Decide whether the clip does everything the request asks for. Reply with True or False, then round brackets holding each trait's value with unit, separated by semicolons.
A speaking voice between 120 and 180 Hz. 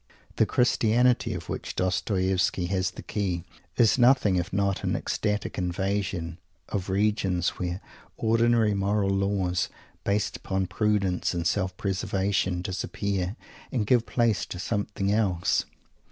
False (100 Hz)